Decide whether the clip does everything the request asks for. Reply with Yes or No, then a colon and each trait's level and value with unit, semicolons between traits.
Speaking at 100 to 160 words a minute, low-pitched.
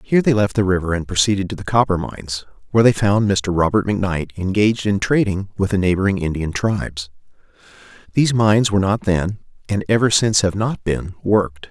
No: average, 190 wpm; low, 100 Hz